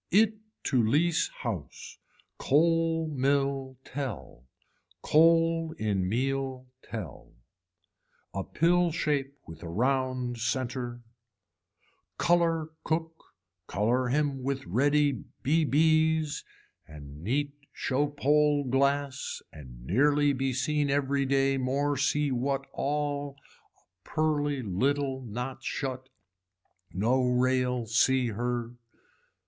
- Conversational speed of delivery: No, slow, 100 wpm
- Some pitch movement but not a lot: Yes, average, 3.1 semitones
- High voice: No, low, 135 Hz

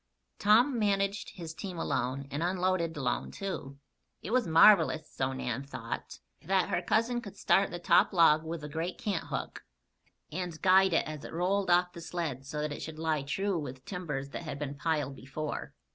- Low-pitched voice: No, medium, 165 Hz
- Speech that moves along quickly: No, average, 185 wpm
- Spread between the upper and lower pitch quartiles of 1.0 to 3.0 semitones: No, average, 4.2 semitones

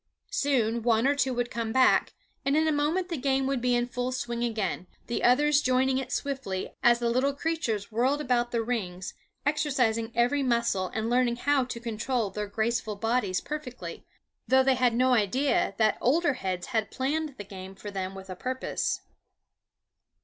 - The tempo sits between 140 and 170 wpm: No, average, 180 wpm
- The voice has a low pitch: No, high, 245 Hz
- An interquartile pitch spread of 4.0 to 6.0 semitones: No, average, 3.3 semitones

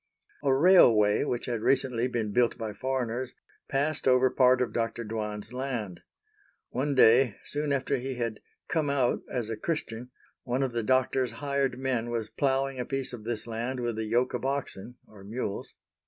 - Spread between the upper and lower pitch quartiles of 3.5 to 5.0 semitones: No, average, 2.7 semitones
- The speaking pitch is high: No, low, 125 Hz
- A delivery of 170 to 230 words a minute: Yes, average, 175 wpm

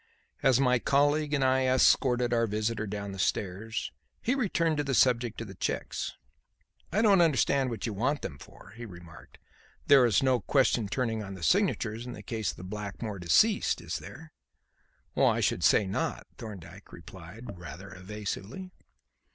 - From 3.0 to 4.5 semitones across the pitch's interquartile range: No, average, 5.1 semitones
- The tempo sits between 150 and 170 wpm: Yes, average, 160 wpm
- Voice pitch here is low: Yes, low, 115 Hz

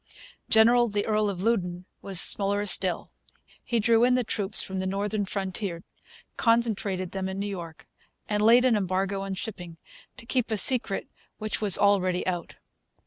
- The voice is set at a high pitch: Yes, high, 200 Hz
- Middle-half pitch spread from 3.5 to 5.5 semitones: No, average, 2.8 semitones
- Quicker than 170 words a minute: No, average, 165 wpm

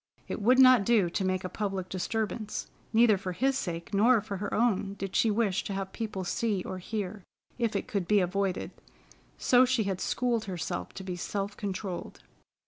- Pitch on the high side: Yes, high, 200 Hz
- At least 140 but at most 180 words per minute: No, average, 190 wpm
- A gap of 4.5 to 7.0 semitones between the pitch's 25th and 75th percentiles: No, average, 3.1 semitones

